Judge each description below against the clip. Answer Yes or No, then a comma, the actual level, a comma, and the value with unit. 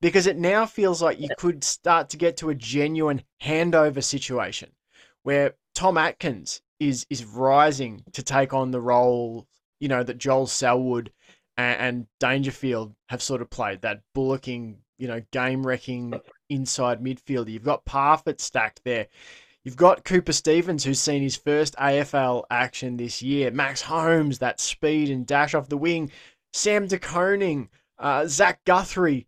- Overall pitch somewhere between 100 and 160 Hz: Yes, low, 135 Hz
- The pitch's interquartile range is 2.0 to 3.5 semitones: No, average, 3.9 semitones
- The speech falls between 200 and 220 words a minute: No, average, 155 wpm